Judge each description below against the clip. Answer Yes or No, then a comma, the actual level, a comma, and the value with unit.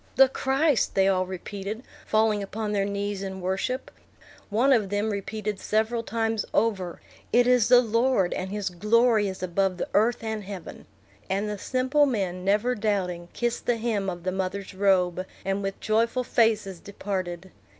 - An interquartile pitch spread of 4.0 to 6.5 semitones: No, average, 3.1 semitones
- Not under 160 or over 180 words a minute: Yes, average, 165 wpm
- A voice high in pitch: Yes, high, 205 Hz